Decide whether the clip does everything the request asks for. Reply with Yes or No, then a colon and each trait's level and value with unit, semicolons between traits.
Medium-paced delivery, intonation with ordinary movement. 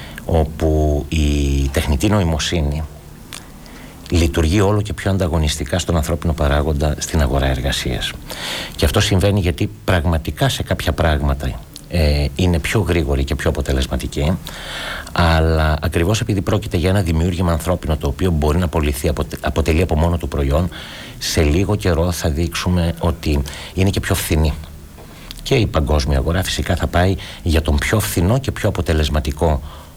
Yes: average, 145 wpm; average, 3.5 semitones